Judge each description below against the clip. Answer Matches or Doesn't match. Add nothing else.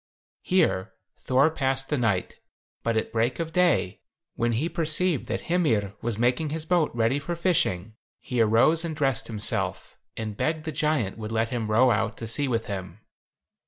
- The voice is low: Matches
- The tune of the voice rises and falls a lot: Matches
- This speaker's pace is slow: Doesn't match